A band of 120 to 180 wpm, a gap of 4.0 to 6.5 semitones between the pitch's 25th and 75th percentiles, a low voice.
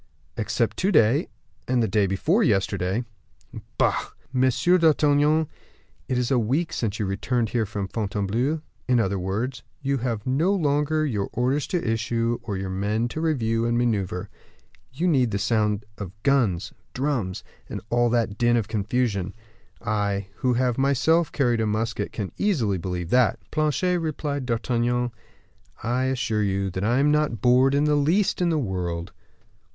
Yes: average, 160 wpm; average, 5.1 semitones; low, 120 Hz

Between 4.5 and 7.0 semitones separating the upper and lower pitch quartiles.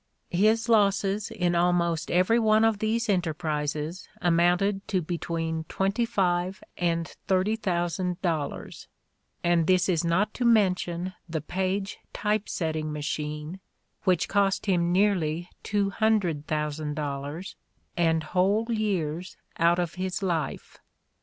No: average, 3.5 semitones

